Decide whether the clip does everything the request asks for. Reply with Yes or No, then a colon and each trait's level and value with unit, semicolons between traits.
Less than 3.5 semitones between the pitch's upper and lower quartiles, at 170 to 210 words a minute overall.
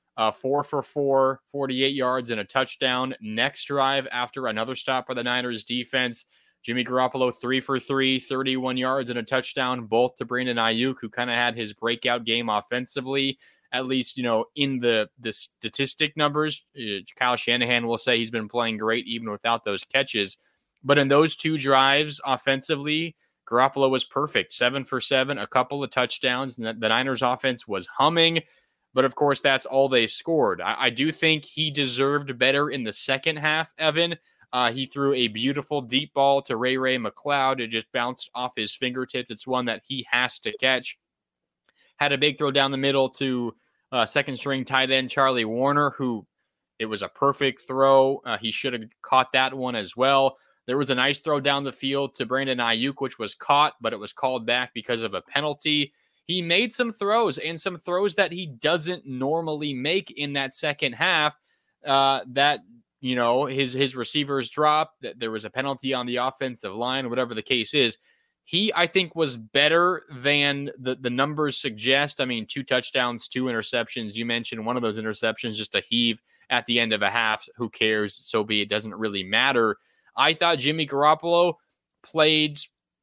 Yes: average, 2.8 semitones; average, 190 wpm